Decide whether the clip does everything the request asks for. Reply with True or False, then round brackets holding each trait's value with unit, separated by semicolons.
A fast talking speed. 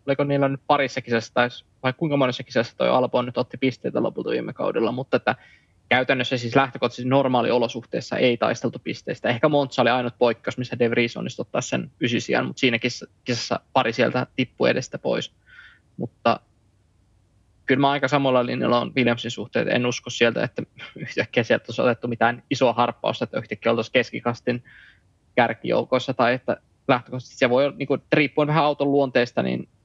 True (170 wpm)